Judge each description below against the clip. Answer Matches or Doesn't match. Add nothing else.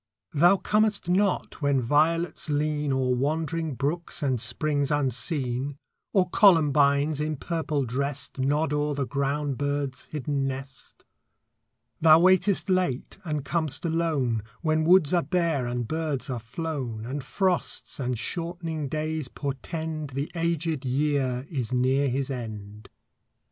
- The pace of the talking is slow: Matches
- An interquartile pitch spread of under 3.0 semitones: Doesn't match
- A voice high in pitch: Doesn't match